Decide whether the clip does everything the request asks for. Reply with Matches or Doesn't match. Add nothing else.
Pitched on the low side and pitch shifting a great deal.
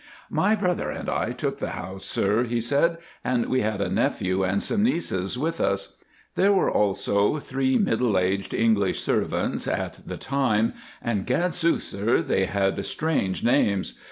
Matches